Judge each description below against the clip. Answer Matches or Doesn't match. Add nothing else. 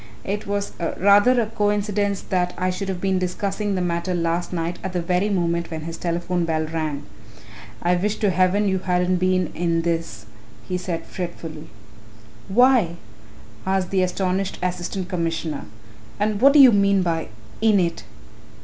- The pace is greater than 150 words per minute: Matches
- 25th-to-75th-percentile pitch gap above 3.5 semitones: Doesn't match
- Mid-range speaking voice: Matches